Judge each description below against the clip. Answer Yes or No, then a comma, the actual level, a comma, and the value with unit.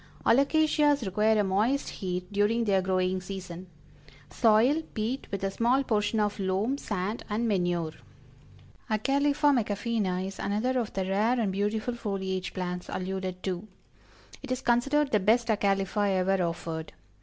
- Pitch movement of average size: Yes, average, 3.9 semitones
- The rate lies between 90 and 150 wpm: Yes, average, 145 wpm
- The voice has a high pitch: Yes, high, 205 Hz